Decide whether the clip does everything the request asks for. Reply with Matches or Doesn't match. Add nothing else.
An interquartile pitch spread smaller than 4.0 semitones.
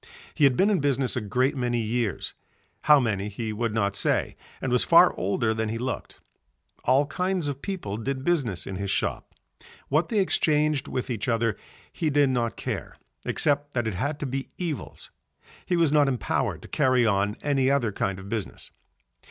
Doesn't match